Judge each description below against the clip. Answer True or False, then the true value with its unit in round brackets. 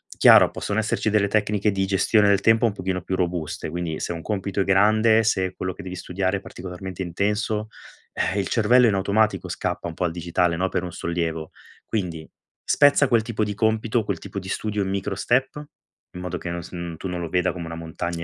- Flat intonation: False (3.3 semitones)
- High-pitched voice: False (95 Hz)